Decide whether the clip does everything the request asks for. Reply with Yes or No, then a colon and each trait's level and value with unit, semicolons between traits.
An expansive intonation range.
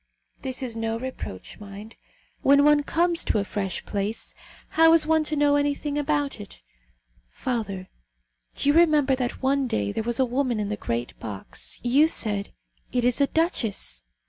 Yes: wide, 5.7 semitones